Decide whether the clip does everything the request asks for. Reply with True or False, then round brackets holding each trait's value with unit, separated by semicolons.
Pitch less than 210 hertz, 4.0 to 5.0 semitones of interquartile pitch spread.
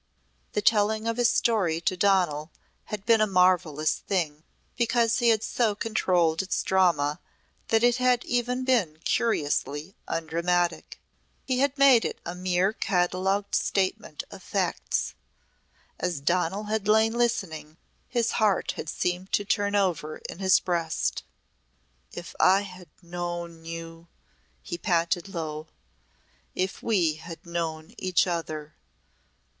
True (185 Hz; 4.4 semitones)